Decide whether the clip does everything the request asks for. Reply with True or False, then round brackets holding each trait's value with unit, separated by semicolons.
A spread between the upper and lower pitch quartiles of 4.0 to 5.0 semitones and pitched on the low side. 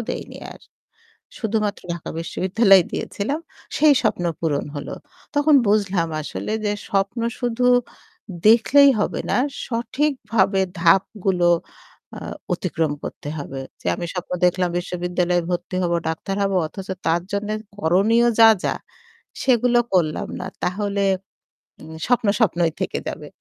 False (4.4 semitones; 195 Hz)